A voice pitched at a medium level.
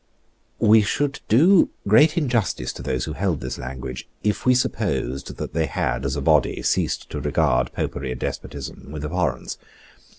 No: very low, 80 Hz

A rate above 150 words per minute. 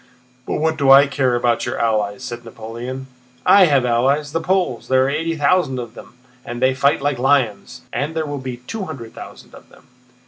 Yes: average, 200 wpm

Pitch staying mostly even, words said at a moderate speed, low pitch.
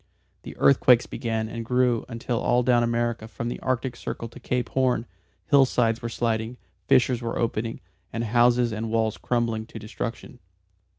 Yes: narrow, 1.4 semitones; average, 160 wpm; low, 120 Hz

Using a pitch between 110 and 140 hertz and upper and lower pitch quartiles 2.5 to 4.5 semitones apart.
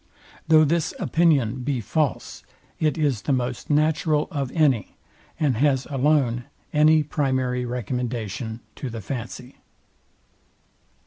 Yes: low, 135 Hz; average, 3.7 semitones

